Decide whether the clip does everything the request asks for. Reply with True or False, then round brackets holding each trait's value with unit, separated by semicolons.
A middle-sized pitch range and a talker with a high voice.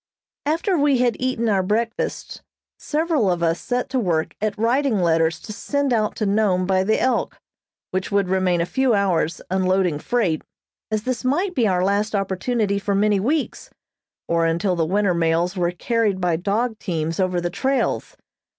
True (4.9 semitones; 200 Hz)